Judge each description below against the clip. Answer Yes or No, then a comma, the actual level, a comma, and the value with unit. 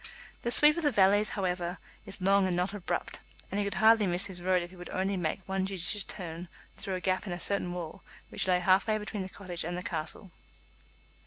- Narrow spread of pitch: Yes, narrow, 2.1 semitones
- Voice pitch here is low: No, high, 190 Hz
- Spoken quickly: Yes, fast, 230 wpm